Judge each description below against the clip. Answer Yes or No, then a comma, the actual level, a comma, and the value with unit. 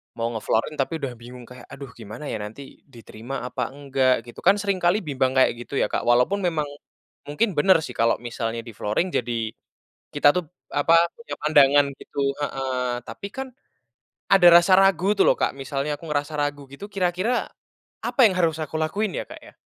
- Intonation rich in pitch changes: Yes, wide, 5.8 semitones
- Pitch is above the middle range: No, medium, 145 Hz